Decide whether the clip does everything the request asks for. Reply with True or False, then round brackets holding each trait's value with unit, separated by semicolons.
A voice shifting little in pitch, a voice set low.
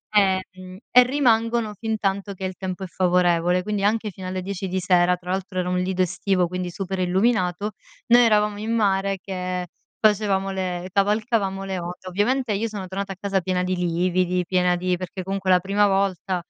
False (2.0 semitones; 190 Hz)